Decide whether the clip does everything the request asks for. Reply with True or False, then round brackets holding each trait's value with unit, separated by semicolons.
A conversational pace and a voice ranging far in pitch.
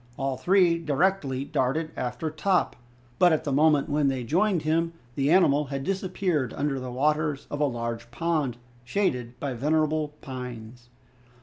False (150 wpm; 4.1 semitones)